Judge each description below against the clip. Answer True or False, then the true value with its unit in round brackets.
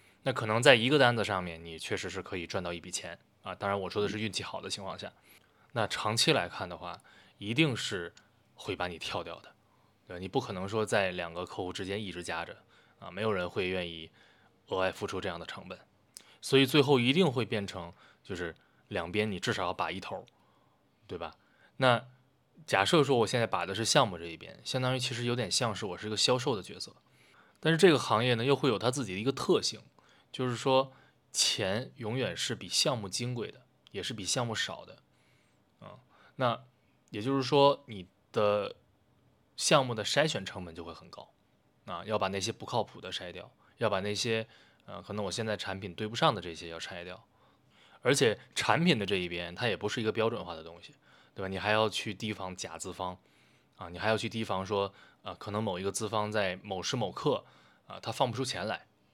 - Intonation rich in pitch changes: False (4.7 semitones)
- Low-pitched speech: True (105 Hz)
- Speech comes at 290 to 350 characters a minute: True (295 characters per minute)